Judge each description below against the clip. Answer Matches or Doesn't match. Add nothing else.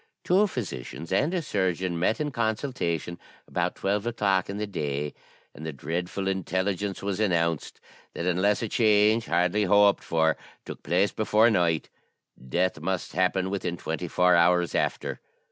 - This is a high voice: Doesn't match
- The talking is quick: Doesn't match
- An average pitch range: Matches